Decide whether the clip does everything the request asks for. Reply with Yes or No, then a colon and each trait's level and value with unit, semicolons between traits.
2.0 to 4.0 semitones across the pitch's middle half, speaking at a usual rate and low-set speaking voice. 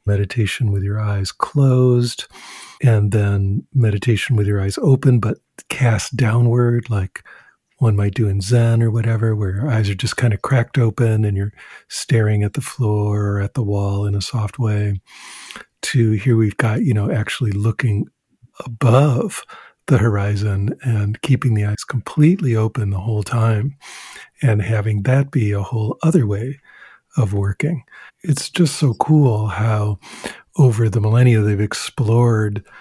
Yes: average, 3.4 semitones; average, 155 wpm; low, 115 Hz